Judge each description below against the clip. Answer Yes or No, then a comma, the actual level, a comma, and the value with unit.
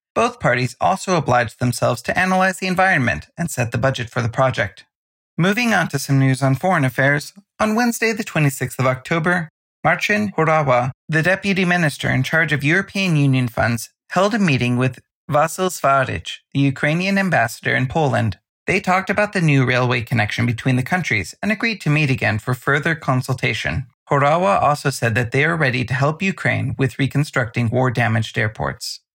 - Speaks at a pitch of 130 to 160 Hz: Yes, medium, 140 Hz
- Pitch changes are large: Yes, wide, 6.0 semitones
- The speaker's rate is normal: Yes, average, 175 wpm